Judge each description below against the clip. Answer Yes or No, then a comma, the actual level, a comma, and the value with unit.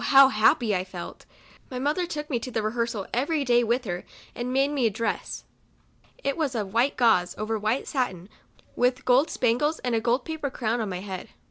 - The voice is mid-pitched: No, high, 240 Hz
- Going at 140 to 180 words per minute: No, fast, 205 wpm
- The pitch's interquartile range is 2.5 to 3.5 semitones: No, average, 3.9 semitones